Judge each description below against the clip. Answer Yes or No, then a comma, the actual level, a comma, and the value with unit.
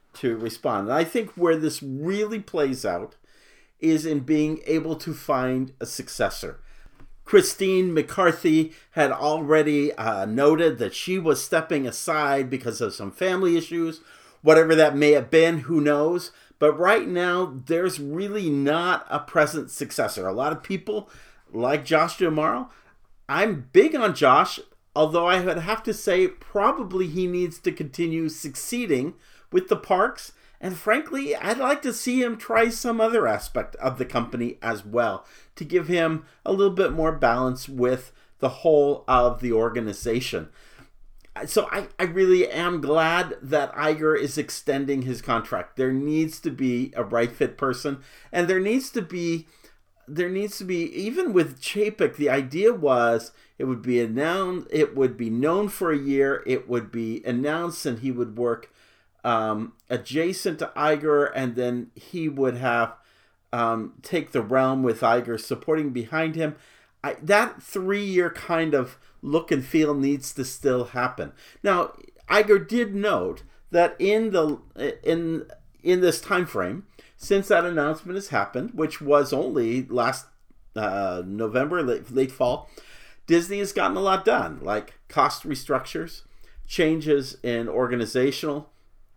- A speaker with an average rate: Yes, average, 155 wpm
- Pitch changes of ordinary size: No, wide, 5.9 semitones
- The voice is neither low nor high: Yes, medium, 155 Hz